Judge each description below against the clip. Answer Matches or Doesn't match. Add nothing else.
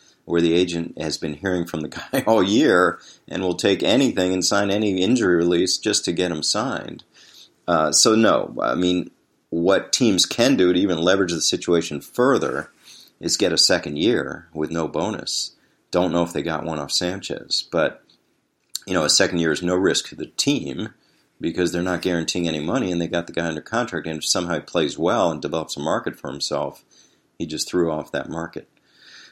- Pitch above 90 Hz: Doesn't match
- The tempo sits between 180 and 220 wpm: Matches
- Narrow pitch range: Matches